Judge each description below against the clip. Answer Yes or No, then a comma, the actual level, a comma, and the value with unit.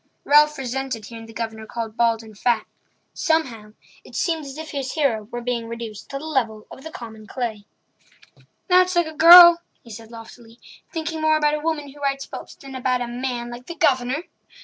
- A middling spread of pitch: Yes, average, 4.9 semitones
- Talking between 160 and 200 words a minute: Yes, average, 195 wpm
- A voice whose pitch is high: Yes, very high, 255 Hz